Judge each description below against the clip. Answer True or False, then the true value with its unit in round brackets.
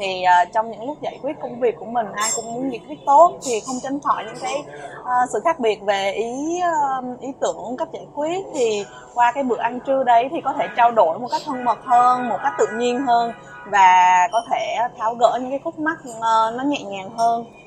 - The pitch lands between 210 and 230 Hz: False (245 Hz)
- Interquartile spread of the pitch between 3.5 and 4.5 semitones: True (4.2 semitones)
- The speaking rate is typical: True (225 wpm)